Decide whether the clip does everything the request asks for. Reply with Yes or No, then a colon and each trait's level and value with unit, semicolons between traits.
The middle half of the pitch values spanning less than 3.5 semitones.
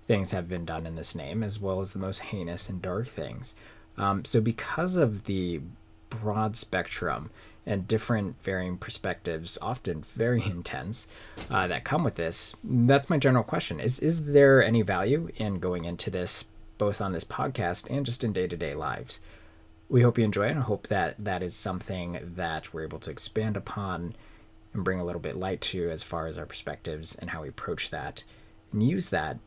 No: average, 4.5 semitones